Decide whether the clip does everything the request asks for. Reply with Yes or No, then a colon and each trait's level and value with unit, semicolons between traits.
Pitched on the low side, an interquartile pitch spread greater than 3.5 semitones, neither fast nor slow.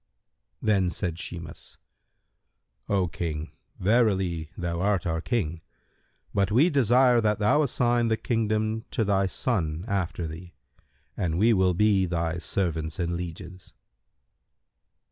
No: very low, 95 Hz; average, 4.4 semitones; slow, 125 wpm